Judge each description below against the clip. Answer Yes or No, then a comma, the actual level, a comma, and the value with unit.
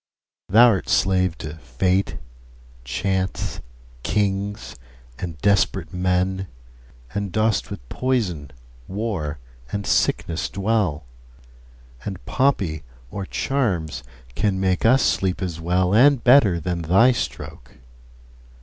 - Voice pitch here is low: Yes, very low, 95 Hz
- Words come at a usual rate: No, slow, 105 wpm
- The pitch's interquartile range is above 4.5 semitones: No, average, 3.6 semitones